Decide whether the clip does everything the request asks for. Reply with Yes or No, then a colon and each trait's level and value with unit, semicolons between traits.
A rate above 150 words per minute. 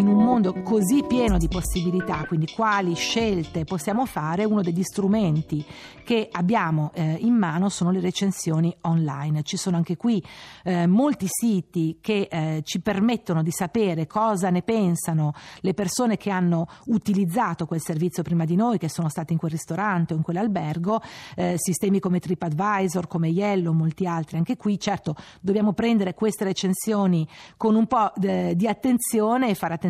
Yes: average, 165 wpm